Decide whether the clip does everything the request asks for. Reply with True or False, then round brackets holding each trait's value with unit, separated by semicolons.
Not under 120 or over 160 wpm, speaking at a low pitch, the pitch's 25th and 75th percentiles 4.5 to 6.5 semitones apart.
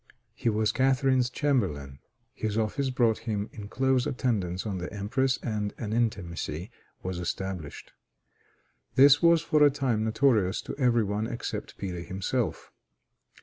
True (140 wpm; 110 Hz; 5.3 semitones)